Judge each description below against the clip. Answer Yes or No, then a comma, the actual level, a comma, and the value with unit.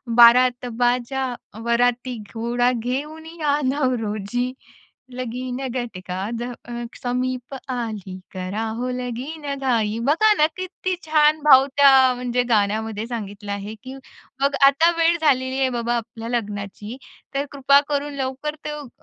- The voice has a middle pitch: No, very high, 250 Hz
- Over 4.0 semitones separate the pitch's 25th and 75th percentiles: No, average, 3.3 semitones